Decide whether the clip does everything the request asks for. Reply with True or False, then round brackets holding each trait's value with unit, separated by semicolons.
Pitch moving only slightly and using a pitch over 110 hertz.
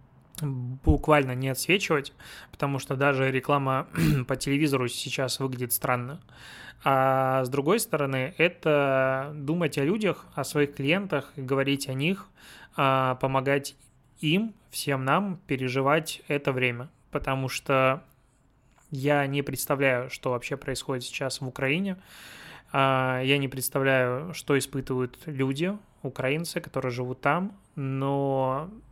True (2.0 semitones; 135 Hz)